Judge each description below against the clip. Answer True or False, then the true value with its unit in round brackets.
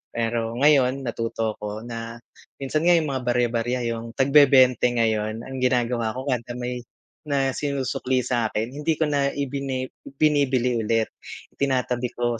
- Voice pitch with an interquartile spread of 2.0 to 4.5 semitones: True (2.8 semitones)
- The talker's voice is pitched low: True (125 Hz)